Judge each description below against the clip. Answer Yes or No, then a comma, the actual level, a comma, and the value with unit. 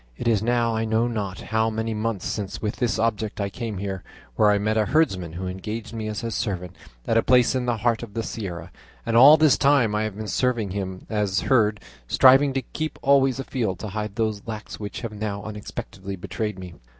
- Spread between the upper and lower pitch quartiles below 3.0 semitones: Yes, narrow, 2.6 semitones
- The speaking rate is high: Yes, fast, 220 wpm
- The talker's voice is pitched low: Yes, low, 110 Hz